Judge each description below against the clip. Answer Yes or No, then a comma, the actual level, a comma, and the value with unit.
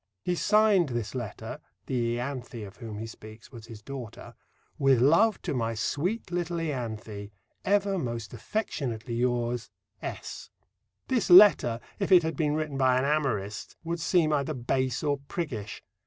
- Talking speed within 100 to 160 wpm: Yes, average, 155 wpm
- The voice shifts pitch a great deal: Yes, wide, 6.1 semitones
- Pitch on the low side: Yes, low, 130 Hz